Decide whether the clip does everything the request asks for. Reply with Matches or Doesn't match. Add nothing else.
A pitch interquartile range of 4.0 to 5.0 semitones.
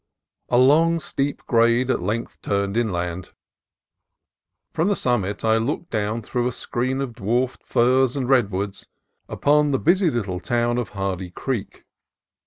Matches